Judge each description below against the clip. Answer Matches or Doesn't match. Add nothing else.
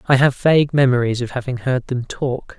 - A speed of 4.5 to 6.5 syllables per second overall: Matches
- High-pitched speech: Doesn't match